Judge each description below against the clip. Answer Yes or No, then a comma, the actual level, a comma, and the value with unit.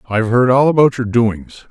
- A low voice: Yes, low, 120 Hz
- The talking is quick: Yes, fast, 210 wpm